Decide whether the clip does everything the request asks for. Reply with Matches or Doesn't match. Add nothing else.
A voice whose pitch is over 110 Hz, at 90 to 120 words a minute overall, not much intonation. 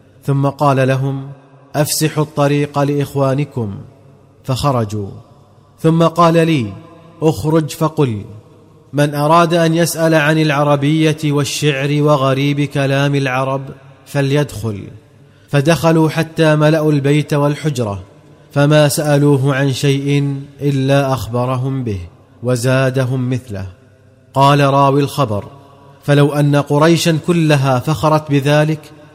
Matches